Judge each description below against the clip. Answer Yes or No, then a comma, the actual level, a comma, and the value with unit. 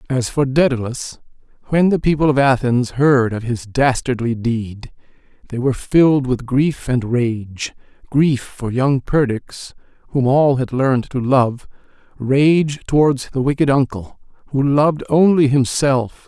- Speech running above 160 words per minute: No, average, 140 wpm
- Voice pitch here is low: Yes, low, 130 Hz